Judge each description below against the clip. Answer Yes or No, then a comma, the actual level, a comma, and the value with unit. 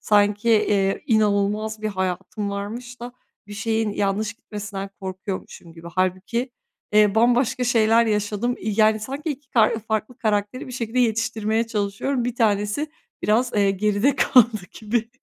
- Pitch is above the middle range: Yes, high, 215 Hz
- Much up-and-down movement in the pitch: No, narrow, 2.6 semitones